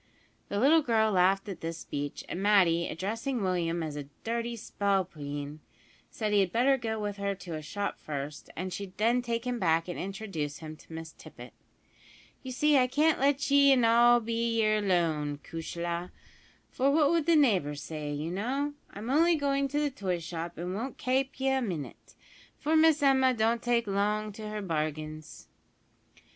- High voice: Yes, high, 210 Hz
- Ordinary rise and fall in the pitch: No, wide, 7.0 semitones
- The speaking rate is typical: Yes, average, 180 wpm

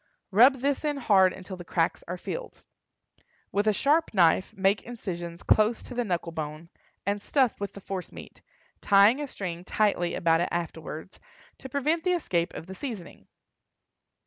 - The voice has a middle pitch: No, high, 200 Hz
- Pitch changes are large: Yes, wide, 6.0 semitones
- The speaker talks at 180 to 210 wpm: No, average, 170 wpm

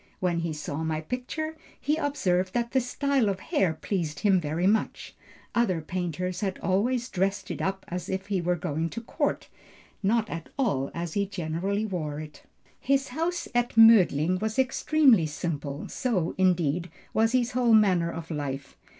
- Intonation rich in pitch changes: Yes, wide, 5.8 semitones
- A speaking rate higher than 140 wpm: Yes, average, 165 wpm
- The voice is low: No, medium, 185 Hz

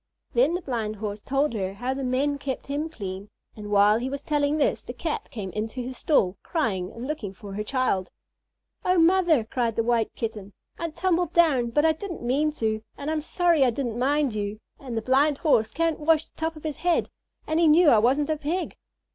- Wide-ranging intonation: Yes, wide, 6.0 semitones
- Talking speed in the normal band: No, fast, 220 wpm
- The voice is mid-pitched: No, very high, 270 Hz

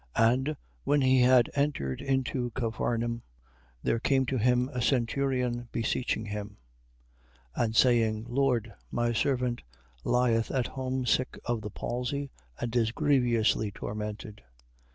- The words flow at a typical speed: No, slow, 130 wpm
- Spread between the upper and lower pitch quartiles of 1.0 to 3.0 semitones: Yes, narrow, 2.4 semitones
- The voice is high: No, low, 120 Hz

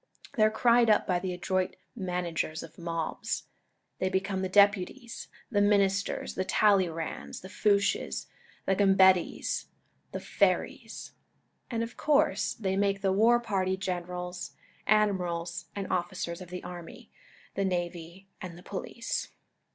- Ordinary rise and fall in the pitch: No, narrow, 2.3 semitones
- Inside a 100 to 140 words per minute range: Yes, slow, 135 wpm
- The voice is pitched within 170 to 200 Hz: Yes, high, 190 Hz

